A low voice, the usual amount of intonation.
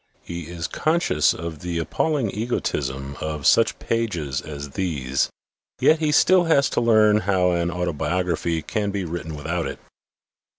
No: very low, 85 Hz; wide, 5.7 semitones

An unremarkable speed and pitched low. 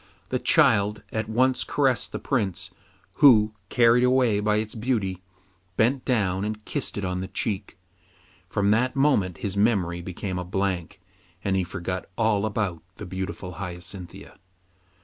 Yes: average, 150 wpm; low, 105 Hz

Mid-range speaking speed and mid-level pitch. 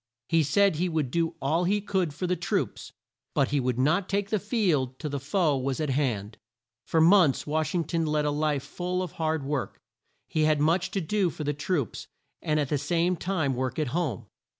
No: fast, 215 wpm; medium, 155 Hz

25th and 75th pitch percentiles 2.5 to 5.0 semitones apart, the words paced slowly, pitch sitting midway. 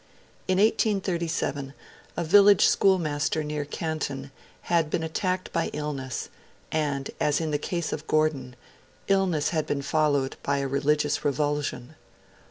Yes: average, 2.9 semitones; slow, 130 wpm; medium, 150 Hz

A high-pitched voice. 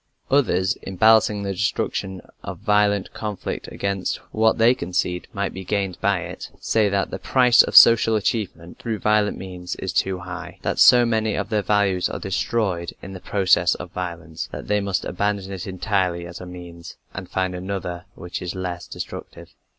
No: very low, 95 Hz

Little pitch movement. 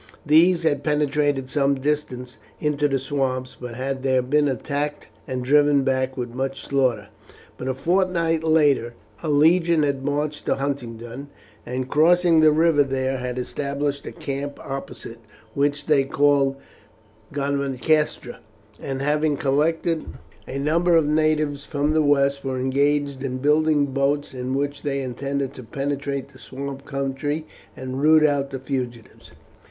Yes: narrow, 2.0 semitones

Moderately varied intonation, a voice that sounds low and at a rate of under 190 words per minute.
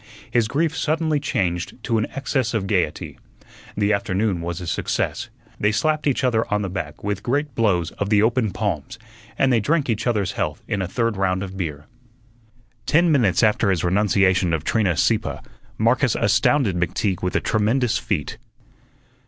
Yes: average, 4.7 semitones; low, 105 Hz; average, 170 wpm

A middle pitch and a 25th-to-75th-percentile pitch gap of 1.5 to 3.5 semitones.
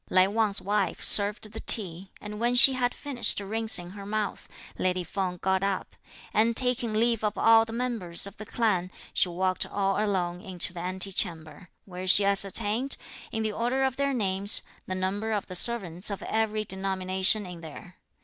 No: high, 200 Hz; average, 3.1 semitones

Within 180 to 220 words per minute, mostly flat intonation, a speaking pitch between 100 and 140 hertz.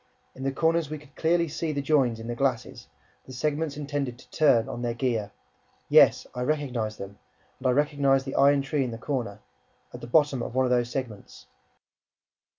No: average, 195 wpm; average, 3.3 semitones; low, 135 Hz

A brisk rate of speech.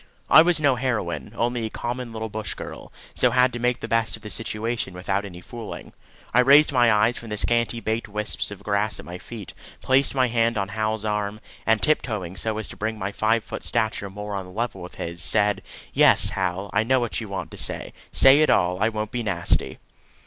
Yes: fast, 220 wpm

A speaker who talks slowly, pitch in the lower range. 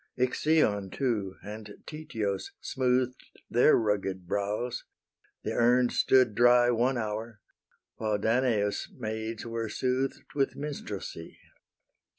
Yes: slow, 105 wpm; low, 115 Hz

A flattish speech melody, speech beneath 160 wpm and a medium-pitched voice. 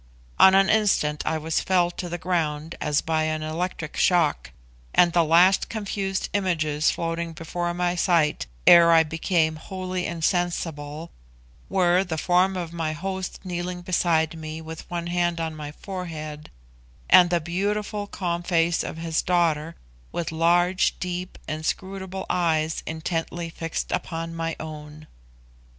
Yes: narrow, 2.1 semitones; average, 140 wpm; medium, 170 Hz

